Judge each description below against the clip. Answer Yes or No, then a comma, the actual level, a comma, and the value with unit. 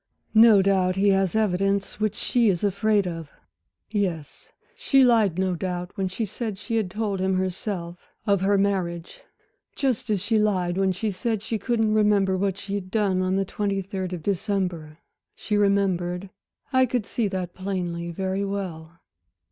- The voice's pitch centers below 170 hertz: No, high, 195 Hz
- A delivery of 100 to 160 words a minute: No, average, 170 wpm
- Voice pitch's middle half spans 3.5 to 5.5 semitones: No, narrow, 2.4 semitones